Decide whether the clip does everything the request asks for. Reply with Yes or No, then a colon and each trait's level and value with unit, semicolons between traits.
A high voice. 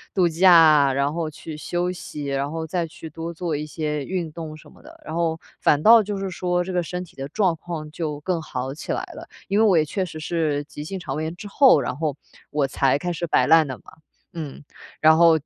No: medium, 160 Hz